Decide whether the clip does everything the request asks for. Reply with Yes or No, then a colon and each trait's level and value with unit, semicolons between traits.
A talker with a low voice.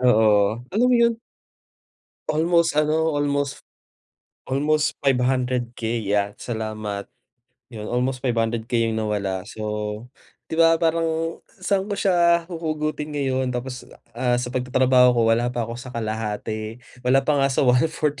Yes: low, 125 Hz